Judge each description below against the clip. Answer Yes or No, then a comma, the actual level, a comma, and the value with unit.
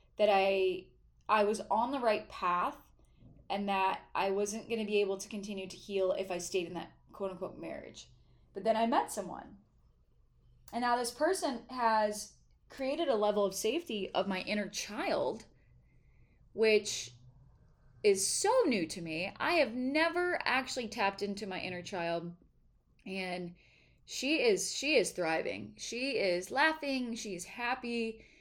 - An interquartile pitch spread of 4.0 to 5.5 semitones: Yes, average, 4.6 semitones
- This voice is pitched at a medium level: No, high, 210 Hz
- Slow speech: No, average, 155 wpm